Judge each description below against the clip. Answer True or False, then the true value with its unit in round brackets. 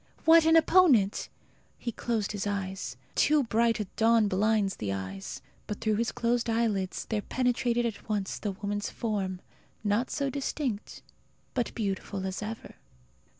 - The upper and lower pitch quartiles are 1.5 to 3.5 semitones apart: True (3.1 semitones)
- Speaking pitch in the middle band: False (215 Hz)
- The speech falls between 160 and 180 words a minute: False (150 wpm)